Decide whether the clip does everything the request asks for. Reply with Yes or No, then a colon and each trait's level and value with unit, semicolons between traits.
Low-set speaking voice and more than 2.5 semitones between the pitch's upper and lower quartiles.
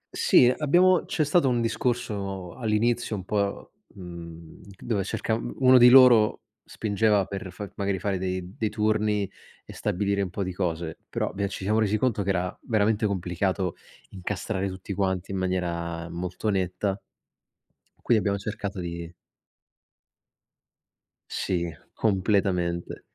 Yes: low, 100 Hz; average, 2.9 semitones